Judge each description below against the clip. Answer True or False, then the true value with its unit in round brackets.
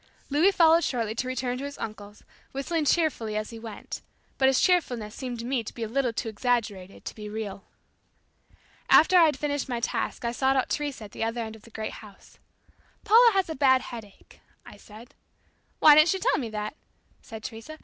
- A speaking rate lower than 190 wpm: False (200 wpm)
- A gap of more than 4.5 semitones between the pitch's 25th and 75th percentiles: True (4.9 semitones)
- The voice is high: True (245 Hz)